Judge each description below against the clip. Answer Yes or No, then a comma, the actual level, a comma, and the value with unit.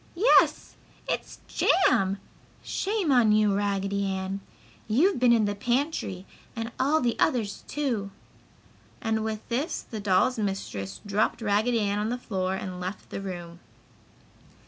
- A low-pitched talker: No, high, 210 Hz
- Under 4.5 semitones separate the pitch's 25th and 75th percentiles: Yes, average, 4.0 semitones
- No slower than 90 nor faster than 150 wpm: Yes, average, 140 wpm